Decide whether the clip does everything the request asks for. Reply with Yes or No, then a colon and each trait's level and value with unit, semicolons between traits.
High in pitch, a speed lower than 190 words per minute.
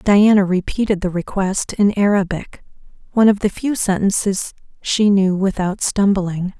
Yes: high, 195 Hz; slow, 135 wpm